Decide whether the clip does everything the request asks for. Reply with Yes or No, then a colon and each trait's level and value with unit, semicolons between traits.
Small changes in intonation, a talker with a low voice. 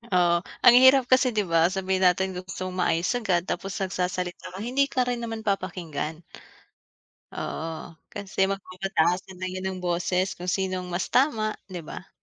No: narrow, 2.2 semitones; medium, 185 Hz